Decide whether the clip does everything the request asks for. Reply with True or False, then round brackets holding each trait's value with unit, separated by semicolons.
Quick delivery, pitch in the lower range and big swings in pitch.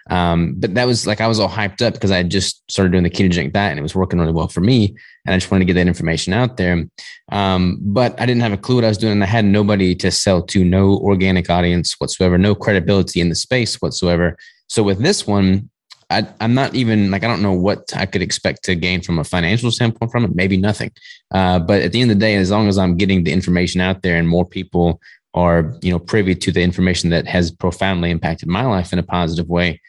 False (255 wpm; 95 Hz; 2.9 semitones)